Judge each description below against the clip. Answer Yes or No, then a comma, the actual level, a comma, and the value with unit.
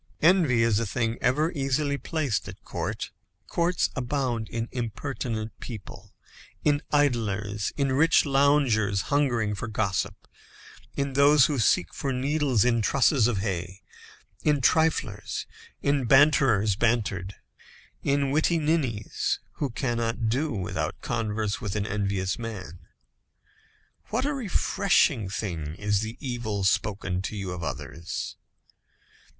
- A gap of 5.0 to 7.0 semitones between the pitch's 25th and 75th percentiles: Yes, wide, 5.5 semitones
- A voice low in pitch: Yes, low, 120 Hz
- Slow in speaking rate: Yes, slow, 125 wpm